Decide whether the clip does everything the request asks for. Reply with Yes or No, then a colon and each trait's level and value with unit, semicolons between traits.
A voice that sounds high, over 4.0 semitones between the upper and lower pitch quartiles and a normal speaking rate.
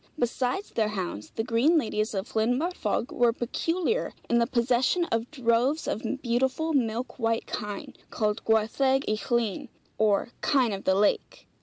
No: high, 235 Hz; average, 3.4 semitones; average, 155 wpm